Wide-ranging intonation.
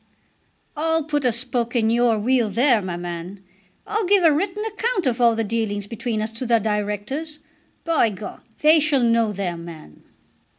Yes: wide, 6.3 semitones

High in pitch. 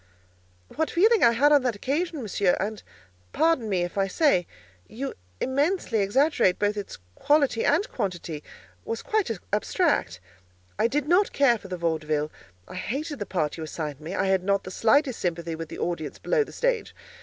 Yes: high, 215 Hz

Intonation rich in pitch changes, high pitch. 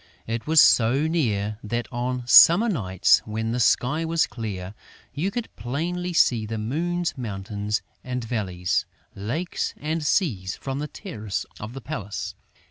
No: wide, 6.9 semitones; low, 120 Hz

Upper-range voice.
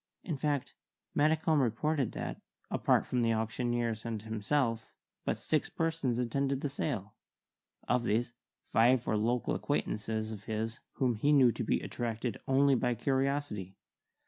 No: low, 120 Hz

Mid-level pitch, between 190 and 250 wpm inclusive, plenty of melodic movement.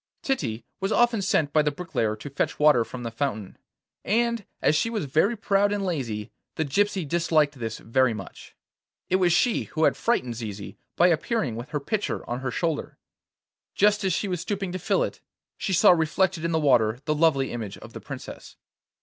Yes: medium, 160 Hz; average, 195 wpm; wide, 7.3 semitones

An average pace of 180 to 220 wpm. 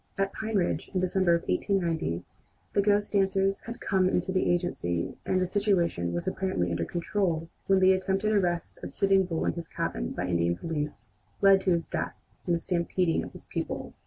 Yes: average, 195 wpm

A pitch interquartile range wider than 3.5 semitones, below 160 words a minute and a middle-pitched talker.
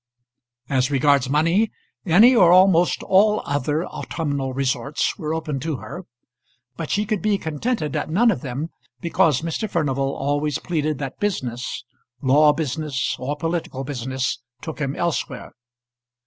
Yes: average, 4.1 semitones; average, 140 wpm; medium, 150 Hz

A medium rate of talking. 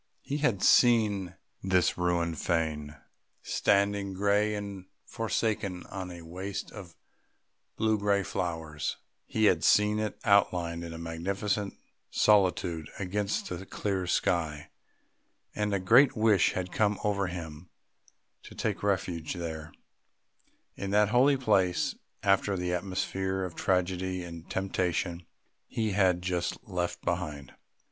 No: slow, 125 wpm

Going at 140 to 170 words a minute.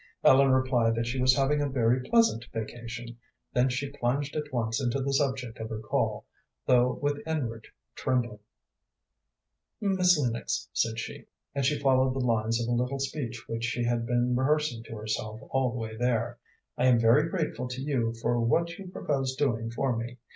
No: average, 185 wpm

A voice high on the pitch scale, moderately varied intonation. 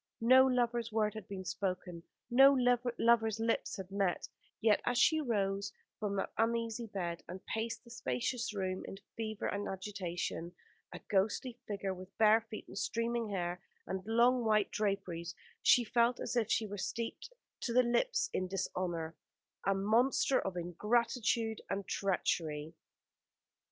Yes: high, 215 Hz; average, 3.7 semitones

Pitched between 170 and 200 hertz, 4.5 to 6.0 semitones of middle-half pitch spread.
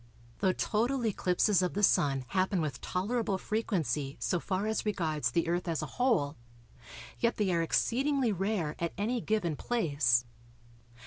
Yes: medium, 185 Hz; wide, 5.5 semitones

